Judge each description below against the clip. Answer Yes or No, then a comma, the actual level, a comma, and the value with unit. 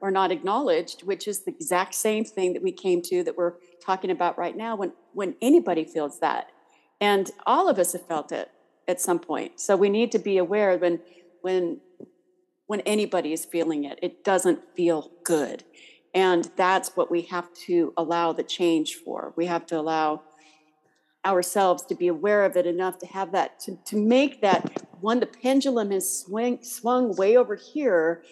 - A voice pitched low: No, medium, 185 Hz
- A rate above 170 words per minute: Yes, average, 185 wpm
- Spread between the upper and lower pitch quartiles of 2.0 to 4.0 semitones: No, average, 4.4 semitones